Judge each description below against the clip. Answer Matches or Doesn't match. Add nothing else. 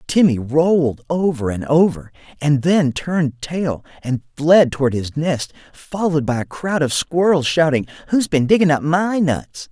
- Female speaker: Doesn't match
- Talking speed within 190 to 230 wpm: Doesn't match